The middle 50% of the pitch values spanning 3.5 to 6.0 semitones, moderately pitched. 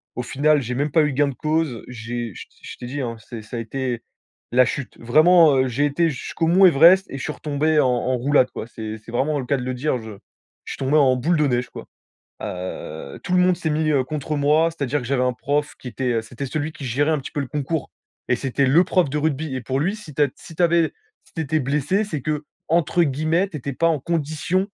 Yes: average, 3.8 semitones; medium, 145 Hz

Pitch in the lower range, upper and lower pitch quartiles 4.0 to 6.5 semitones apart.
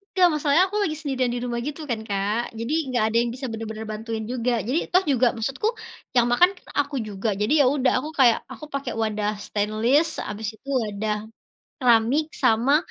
No: high, 240 Hz; average, 4.3 semitones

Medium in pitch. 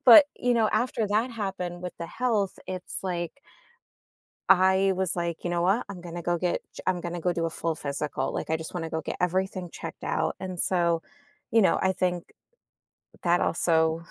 Yes: medium, 180 Hz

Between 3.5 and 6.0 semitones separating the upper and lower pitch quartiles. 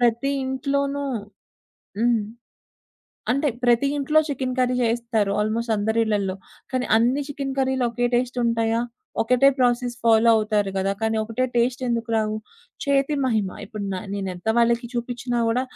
No: narrow, 2.6 semitones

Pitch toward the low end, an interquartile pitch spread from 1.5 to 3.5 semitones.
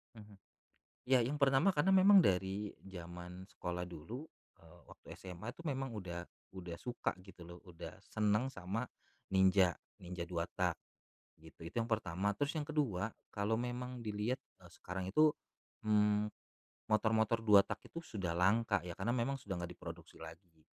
No: low, 105 Hz; average, 5.1 semitones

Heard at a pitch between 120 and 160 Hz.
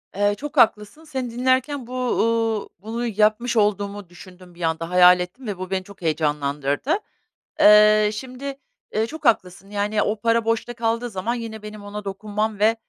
No: high, 210 Hz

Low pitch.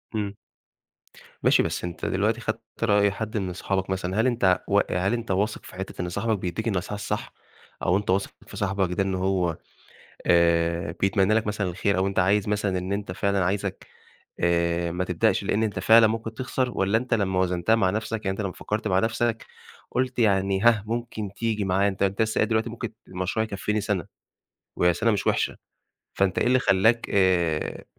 Yes: low, 100 Hz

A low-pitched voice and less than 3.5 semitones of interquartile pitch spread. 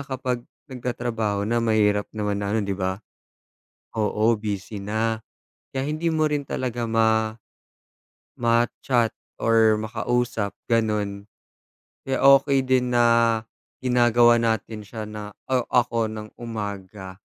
Yes: low, 115 Hz; narrow, 2.5 semitones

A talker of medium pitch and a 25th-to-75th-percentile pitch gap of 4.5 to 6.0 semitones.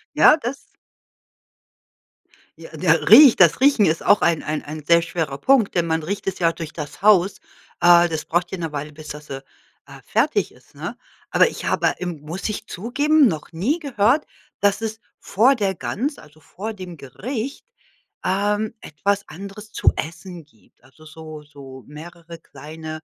Yes: medium, 175 Hz; average, 5.1 semitones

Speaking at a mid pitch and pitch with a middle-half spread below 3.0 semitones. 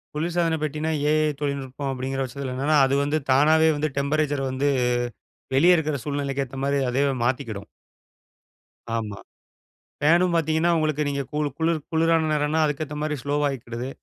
Yes: medium, 145 Hz; narrow, 2.4 semitones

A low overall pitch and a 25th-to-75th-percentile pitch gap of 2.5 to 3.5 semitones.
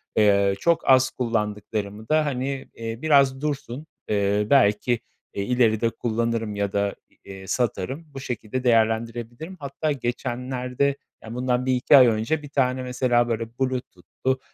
Yes: low, 125 Hz; average, 3.1 semitones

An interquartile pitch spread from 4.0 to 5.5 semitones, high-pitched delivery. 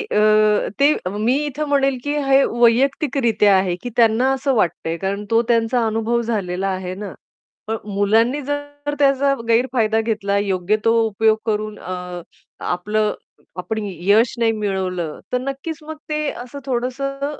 Yes: average, 4.7 semitones; high, 225 Hz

